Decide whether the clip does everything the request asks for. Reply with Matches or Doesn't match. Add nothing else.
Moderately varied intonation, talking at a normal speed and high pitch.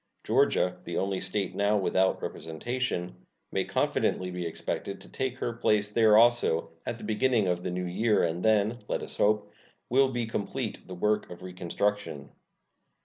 Doesn't match